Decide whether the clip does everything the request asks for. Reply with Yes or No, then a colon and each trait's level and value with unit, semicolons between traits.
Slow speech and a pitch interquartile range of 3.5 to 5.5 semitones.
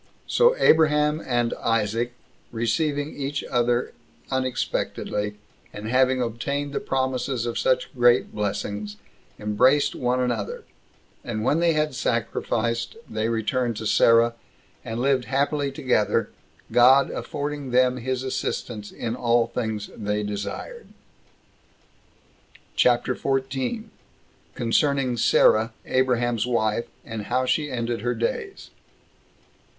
No: slow, 110 wpm; average, 2.8 semitones